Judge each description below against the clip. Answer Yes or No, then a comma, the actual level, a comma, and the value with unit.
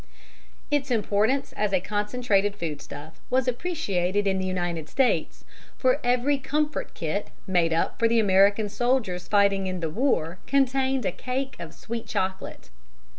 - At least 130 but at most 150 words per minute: Yes, average, 145 wpm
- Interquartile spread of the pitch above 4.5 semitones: Yes, wide, 5.5 semitones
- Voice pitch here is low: No, high, 205 Hz